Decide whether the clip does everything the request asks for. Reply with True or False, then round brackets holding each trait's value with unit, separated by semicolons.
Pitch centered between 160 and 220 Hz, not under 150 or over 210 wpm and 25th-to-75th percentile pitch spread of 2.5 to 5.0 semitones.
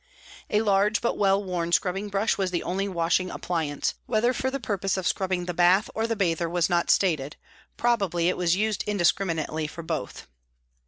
True (185 Hz; 180 wpm; 3.2 semitones)